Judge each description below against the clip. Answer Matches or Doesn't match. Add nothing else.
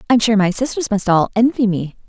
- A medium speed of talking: Doesn't match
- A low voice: Doesn't match